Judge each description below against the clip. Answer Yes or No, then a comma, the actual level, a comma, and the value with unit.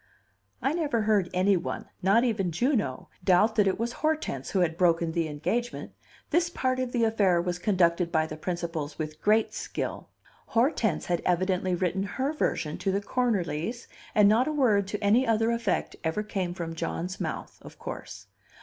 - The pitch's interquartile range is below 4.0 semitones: No, average, 5.1 semitones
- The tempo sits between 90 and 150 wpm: No, average, 175 wpm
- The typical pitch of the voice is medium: No, high, 195 Hz